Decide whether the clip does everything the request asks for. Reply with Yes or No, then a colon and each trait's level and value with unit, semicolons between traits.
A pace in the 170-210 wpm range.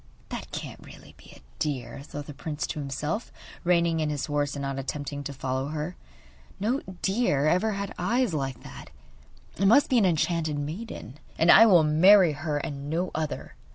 Yes: average, 185 wpm